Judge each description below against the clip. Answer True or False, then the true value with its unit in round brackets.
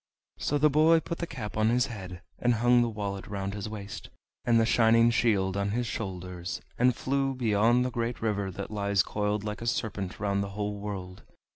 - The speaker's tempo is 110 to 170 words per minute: False (205 wpm)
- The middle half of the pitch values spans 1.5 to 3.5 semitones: True (3.2 semitones)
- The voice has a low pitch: True (105 Hz)